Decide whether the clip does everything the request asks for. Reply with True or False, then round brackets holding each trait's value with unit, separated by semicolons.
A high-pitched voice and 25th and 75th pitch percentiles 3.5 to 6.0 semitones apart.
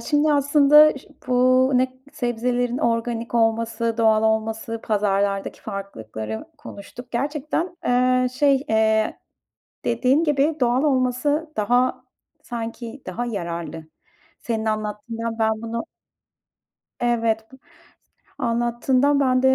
False (240 Hz; 2.9 semitones)